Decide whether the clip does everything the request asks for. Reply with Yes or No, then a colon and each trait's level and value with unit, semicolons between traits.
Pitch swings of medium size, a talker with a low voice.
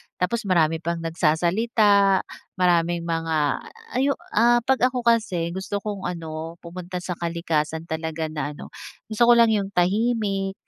No: average, 4.4 semitones; medium, 180 Hz